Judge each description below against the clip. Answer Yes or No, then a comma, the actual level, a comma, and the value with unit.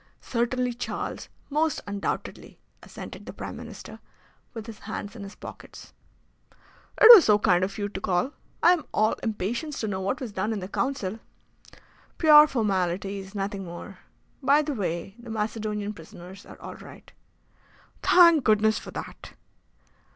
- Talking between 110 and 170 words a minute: Yes, average, 150 wpm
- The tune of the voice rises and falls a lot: No, average, 4.5 semitones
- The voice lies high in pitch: Yes, high, 215 Hz